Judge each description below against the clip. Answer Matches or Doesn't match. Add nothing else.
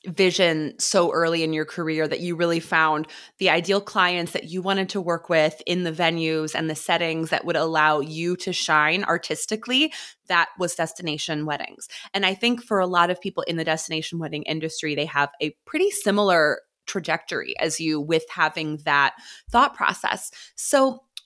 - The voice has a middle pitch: Matches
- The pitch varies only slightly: Doesn't match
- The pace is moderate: Matches